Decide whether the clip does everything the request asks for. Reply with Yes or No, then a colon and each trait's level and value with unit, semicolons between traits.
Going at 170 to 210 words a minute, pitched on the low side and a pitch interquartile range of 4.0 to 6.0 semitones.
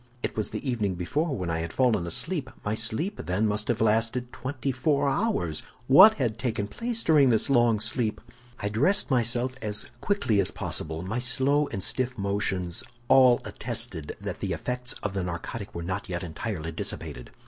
Yes: average, 180 wpm; low, 115 Hz; average, 5.1 semitones